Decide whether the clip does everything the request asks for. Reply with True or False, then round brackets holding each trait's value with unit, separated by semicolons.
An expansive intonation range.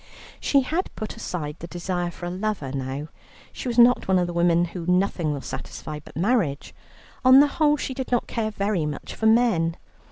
True (6.3 semitones)